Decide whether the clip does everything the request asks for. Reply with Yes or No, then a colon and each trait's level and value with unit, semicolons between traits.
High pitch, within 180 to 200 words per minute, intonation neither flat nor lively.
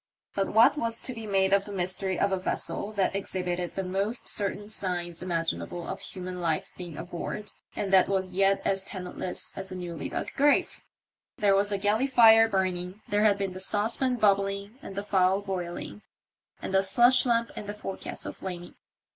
No: high, 195 Hz; average, 185 wpm; narrow, 2.2 semitones